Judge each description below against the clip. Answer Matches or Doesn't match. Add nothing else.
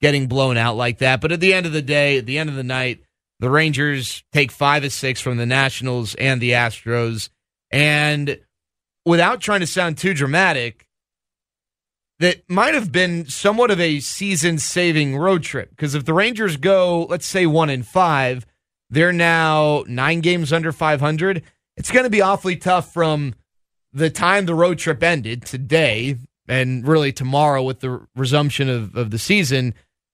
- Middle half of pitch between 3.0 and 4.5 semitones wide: Doesn't match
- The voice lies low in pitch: Doesn't match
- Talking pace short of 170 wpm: Doesn't match